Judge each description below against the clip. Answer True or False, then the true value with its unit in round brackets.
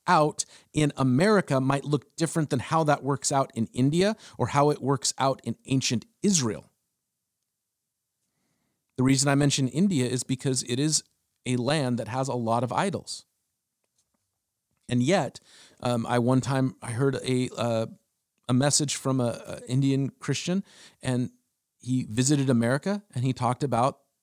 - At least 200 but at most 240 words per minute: False (155 wpm)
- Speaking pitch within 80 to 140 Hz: True (135 Hz)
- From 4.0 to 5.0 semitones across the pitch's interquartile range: False (2.7 semitones)